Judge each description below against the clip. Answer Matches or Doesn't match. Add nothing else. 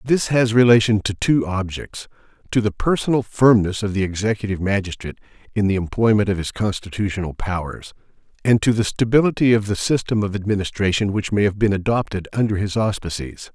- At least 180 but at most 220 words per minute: Doesn't match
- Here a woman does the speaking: Doesn't match